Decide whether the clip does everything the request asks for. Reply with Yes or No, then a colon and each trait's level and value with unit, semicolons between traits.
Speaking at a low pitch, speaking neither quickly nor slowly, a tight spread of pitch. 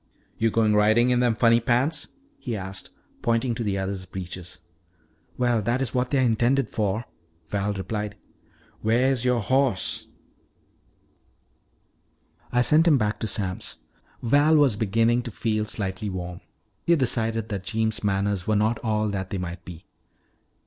No: low, 110 Hz; average, 150 wpm; average, 3.5 semitones